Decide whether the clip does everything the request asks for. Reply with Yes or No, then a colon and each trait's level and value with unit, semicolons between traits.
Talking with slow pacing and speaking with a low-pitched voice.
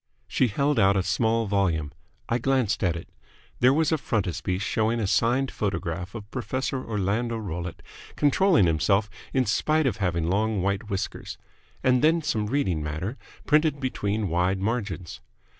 No: average, 155 wpm; low, 105 Hz